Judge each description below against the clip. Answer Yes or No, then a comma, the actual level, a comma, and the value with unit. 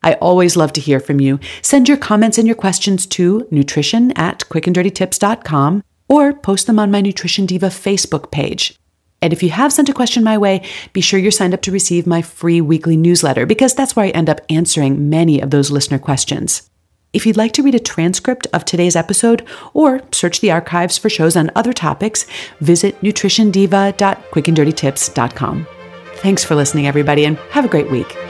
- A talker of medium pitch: Yes, medium, 180 Hz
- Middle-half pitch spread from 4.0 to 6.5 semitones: Yes, wide, 5.4 semitones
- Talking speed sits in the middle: Yes, average, 185 wpm